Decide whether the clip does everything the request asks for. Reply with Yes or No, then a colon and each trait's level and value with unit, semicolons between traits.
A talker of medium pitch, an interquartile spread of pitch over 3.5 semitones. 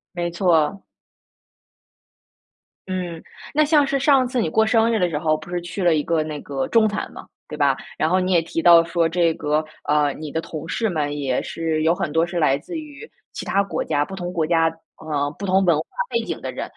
Yes: medium, 170 Hz; average, 3.9 semitones